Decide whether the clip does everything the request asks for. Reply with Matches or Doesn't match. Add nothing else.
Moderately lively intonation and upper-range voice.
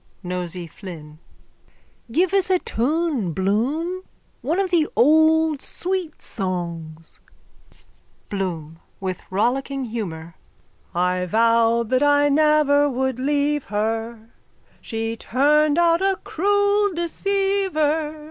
Doesn't match